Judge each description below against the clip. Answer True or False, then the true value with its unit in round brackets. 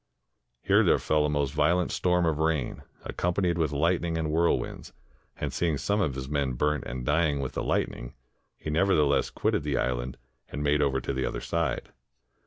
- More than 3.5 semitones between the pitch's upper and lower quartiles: False (3.2 semitones)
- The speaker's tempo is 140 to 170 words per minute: False (185 wpm)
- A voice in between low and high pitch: False (75 Hz)